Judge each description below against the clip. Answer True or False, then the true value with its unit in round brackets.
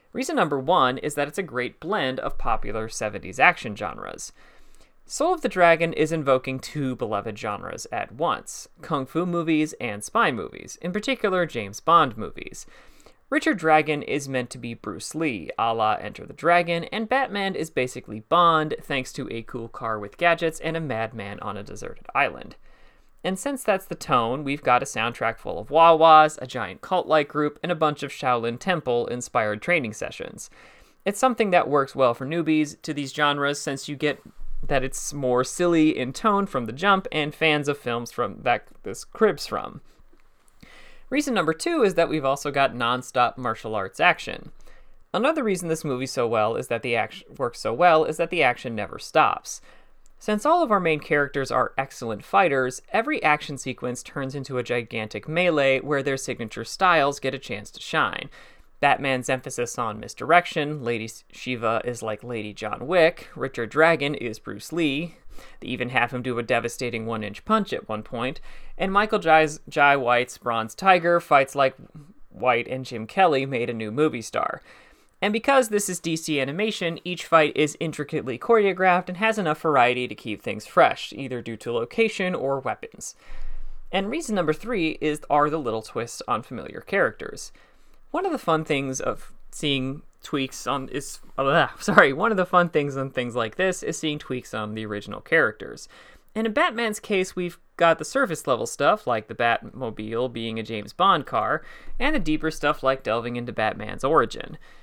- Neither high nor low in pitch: True (145 Hz)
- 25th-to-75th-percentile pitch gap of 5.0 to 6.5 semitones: True (5.6 semitones)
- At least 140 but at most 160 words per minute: False (185 wpm)